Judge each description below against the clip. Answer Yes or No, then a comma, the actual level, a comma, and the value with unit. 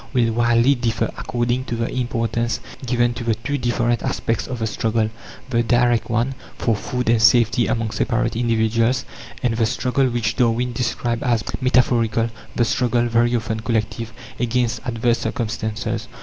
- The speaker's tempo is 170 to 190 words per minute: No, average, 155 wpm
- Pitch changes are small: Yes, narrow, 1.2 semitones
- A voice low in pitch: Yes, low, 120 Hz